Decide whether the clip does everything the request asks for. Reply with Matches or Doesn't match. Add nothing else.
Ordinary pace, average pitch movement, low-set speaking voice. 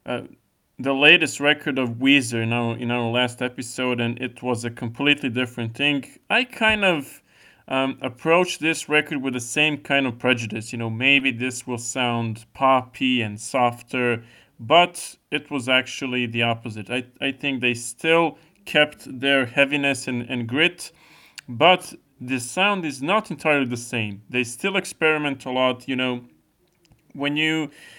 Matches